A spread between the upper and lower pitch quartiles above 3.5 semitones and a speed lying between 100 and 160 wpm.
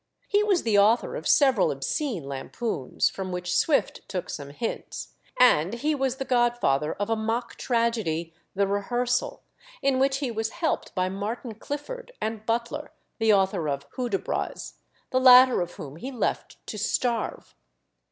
Yes: average, 5.3 semitones; average, 155 wpm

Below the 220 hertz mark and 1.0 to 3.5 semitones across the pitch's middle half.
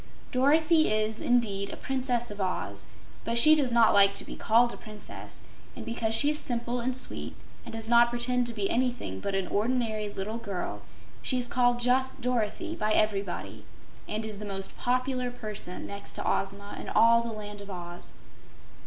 No: high, 230 Hz; average, 3.2 semitones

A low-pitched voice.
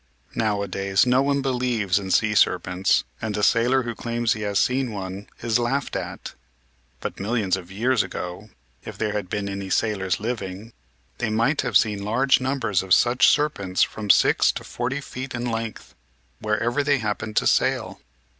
Yes: low, 110 Hz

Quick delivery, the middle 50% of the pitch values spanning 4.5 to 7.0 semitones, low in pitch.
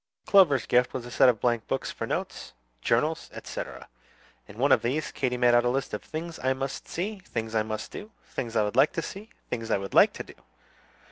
Yes: fast, 225 wpm; average, 5.0 semitones; low, 125 Hz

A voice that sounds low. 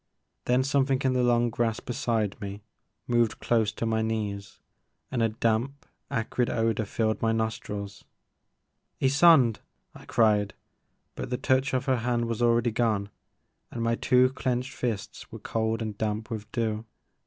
Yes: low, 115 Hz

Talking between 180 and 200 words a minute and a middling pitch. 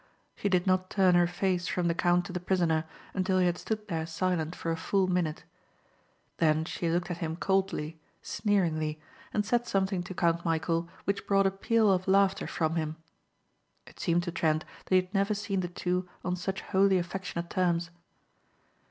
Yes: average, 185 wpm; medium, 180 Hz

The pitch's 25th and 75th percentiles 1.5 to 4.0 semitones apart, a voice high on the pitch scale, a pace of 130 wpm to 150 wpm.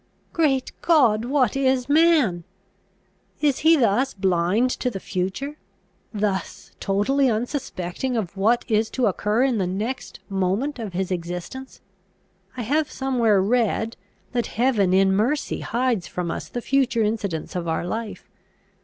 No: wide, 5.4 semitones; high, 225 Hz; average, 140 wpm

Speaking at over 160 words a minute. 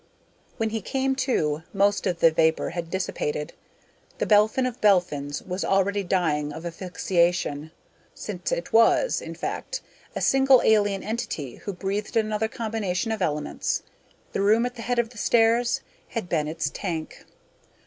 No: average, 155 wpm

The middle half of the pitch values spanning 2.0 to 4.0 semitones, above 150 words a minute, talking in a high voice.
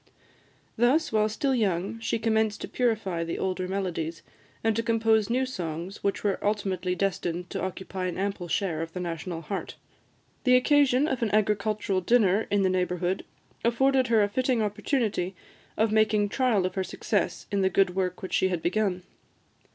Yes: average, 3.6 semitones; average, 175 wpm; high, 200 Hz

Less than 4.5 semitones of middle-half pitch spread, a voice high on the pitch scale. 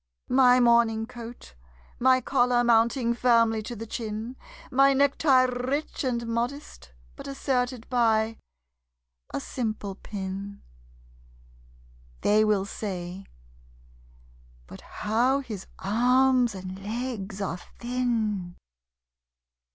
Yes: average, 3.0 semitones; high, 235 Hz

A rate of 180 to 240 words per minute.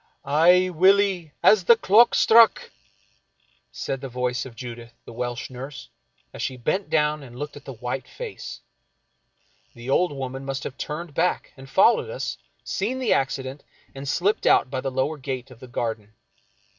No: average, 170 wpm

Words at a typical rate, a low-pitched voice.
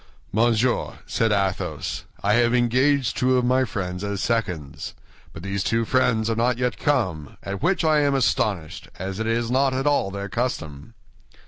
Yes: average, 175 wpm; low, 115 Hz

